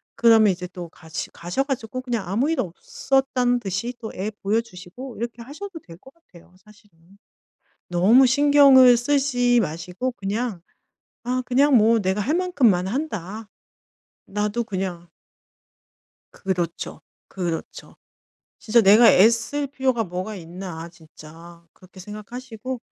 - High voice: Yes, high, 220 Hz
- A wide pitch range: Yes, wide, 5.7 semitones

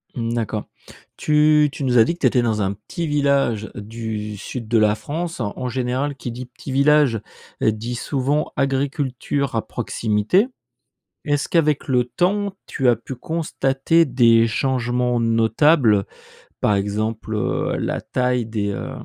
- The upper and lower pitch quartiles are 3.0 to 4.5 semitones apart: Yes, average, 4.2 semitones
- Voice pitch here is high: No, low, 125 Hz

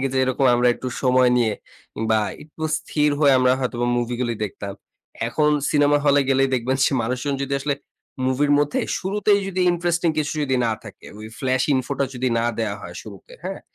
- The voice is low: Yes, low, 130 Hz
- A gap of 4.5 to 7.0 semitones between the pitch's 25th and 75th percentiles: No, average, 3.3 semitones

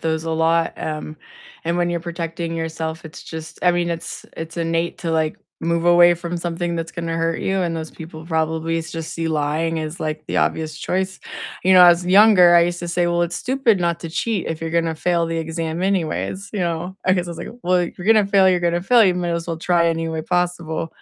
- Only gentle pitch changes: Yes, narrow, 1.5 semitones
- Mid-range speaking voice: Yes, medium, 170 Hz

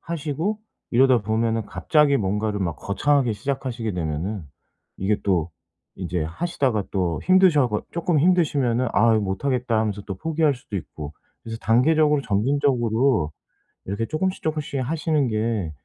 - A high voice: No, low, 115 Hz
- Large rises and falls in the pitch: Yes, wide, 6.2 semitones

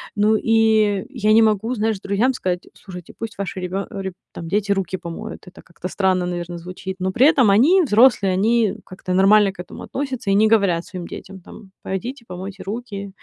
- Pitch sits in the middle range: No, high, 200 Hz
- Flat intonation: No, average, 3.1 semitones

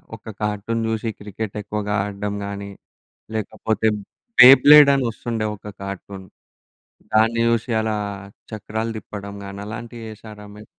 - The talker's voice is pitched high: No, low, 110 Hz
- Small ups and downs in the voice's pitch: Yes, narrow, 1.8 semitones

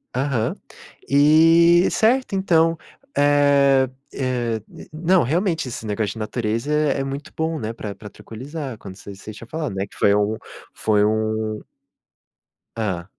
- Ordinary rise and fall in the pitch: No, wide, 6.2 semitones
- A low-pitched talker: Yes, low, 130 Hz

